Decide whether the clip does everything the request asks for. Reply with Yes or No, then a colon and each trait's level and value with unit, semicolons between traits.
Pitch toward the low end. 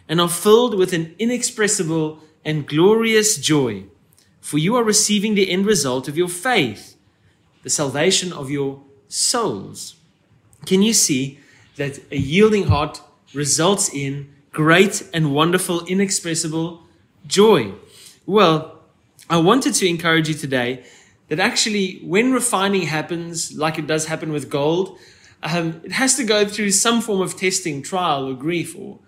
No: medium, 165 Hz